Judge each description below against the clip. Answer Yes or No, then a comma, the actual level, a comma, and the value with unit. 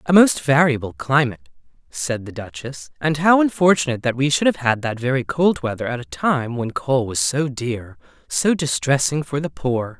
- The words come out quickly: No, average, 190 wpm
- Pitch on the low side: Yes, low, 130 Hz